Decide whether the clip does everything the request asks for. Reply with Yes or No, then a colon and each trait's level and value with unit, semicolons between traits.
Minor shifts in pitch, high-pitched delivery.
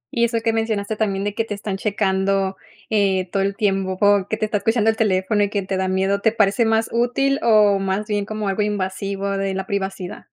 Yes: narrow, 2.1 semitones; high, 200 Hz